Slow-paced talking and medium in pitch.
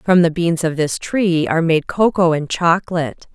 No: average, 195 wpm; medium, 170 Hz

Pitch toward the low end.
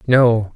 Yes: low, 115 Hz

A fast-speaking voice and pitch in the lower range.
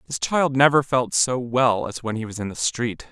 Yes: fast, 250 wpm; low, 115 Hz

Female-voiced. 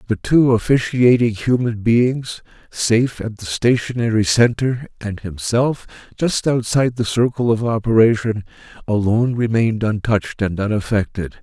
No: male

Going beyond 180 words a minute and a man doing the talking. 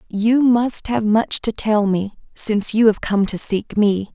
No: fast, 205 wpm; female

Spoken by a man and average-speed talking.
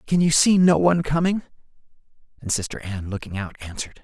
Yes: male; average, 180 wpm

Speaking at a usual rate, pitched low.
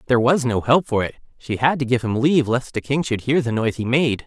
No: fast, 295 wpm; low, 125 Hz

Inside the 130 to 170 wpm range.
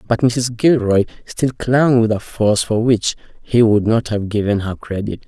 No: average, 195 wpm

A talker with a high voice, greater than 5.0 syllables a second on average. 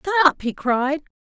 No: very high, 300 Hz; 4.9 syllables/s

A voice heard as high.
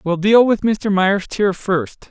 Yes: high, 195 Hz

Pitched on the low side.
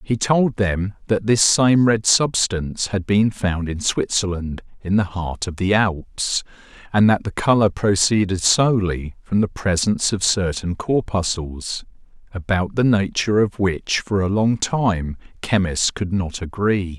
Yes: low, 100 Hz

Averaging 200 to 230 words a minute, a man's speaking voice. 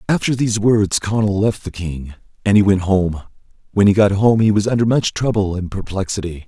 Yes: fast, 205 wpm; male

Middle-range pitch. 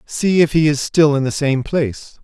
Yes: medium, 150 Hz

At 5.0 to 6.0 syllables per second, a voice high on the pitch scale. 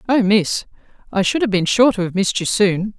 Yes: 5.5 syllables/s; high, 205 Hz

